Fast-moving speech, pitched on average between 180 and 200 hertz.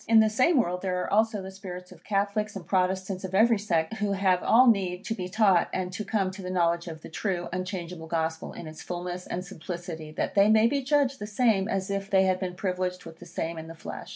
Yes: fast, 245 wpm; medium, 185 Hz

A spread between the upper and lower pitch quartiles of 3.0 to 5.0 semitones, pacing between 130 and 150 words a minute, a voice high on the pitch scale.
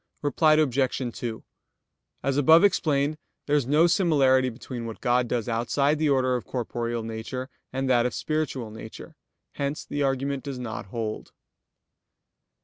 No: average, 3.4 semitones; average, 145 wpm; low, 130 Hz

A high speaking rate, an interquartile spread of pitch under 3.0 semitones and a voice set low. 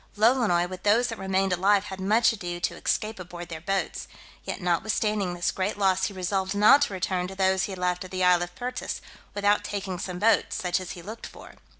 No: fast, 220 wpm; narrow, 2.4 semitones; high, 190 Hz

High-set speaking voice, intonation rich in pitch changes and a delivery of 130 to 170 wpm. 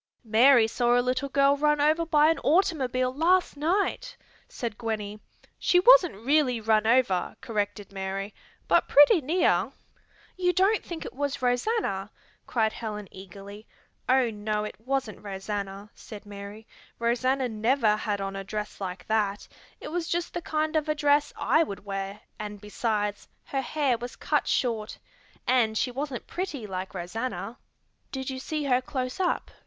Yes: high, 245 Hz; wide, 5.8 semitones; average, 160 wpm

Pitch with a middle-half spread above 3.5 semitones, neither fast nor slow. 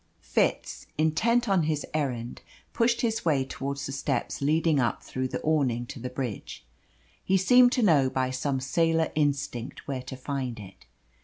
Yes: average, 4.0 semitones; average, 165 wpm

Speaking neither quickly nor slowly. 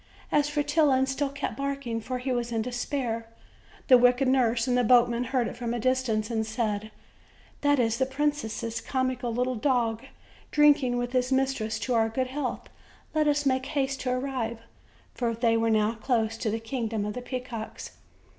Yes: average, 180 wpm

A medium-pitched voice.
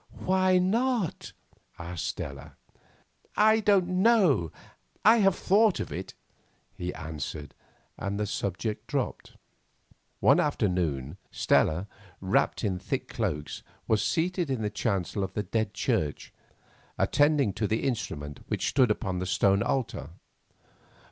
No: low, 105 Hz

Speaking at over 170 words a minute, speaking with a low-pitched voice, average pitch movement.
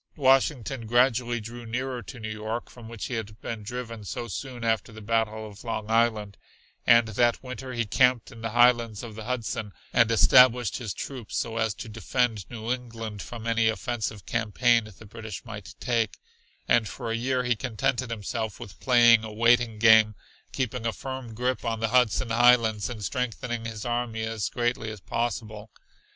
No: average, 180 wpm; low, 115 Hz; narrow, 1.9 semitones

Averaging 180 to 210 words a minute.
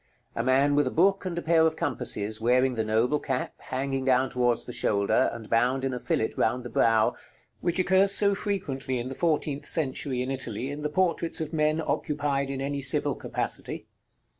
Yes: average, 195 wpm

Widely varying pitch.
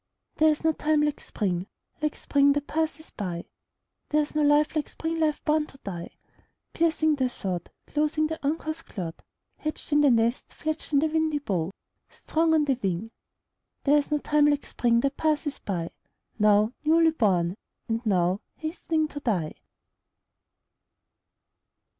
Yes: wide, 6.5 semitones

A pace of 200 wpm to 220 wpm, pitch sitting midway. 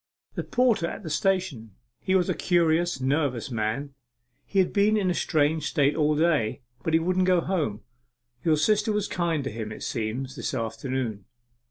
No: average, 180 wpm; medium, 155 Hz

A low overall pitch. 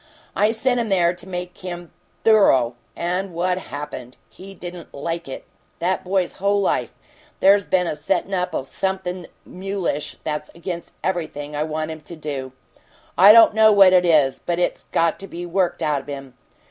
No: medium, 175 Hz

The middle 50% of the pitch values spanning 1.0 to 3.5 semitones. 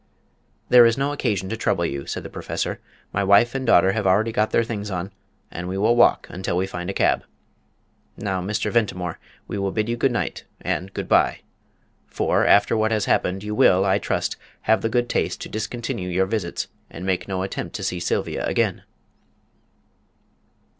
Yes: average, 3.2 semitones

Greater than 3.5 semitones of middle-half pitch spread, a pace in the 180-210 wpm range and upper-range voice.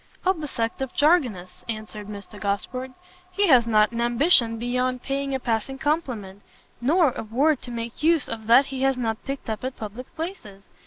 Yes: average, 3.9 semitones; average, 190 wpm; high, 245 Hz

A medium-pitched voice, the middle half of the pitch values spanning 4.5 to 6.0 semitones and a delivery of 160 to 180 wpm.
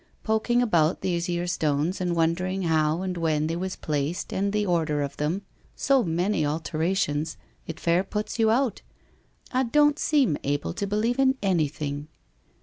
Yes: medium, 175 Hz; average, 5.1 semitones; average, 175 wpm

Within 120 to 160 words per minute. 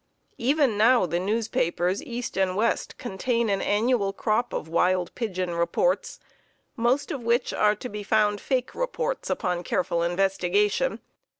Yes: average, 140 wpm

